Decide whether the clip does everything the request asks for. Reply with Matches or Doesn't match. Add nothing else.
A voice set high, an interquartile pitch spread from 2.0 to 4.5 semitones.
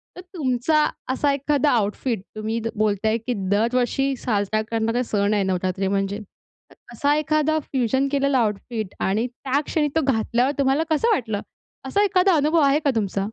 Doesn't match